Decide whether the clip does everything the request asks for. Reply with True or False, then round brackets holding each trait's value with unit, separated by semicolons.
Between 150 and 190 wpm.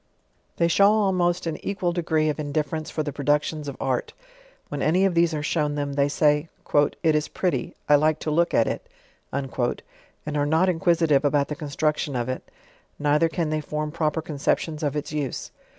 True (185 wpm)